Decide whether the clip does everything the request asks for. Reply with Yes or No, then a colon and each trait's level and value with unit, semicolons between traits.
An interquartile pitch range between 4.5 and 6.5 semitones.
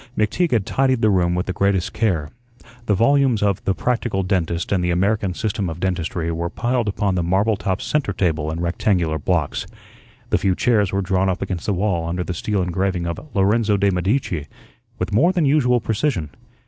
No: average, 3.8 semitones